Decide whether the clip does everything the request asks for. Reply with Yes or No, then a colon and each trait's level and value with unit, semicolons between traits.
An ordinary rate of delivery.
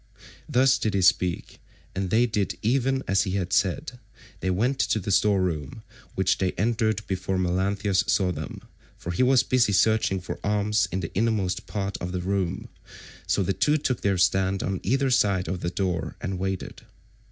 Yes: average, 185 wpm